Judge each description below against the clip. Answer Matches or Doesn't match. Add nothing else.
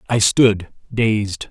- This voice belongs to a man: Matches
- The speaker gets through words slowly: Matches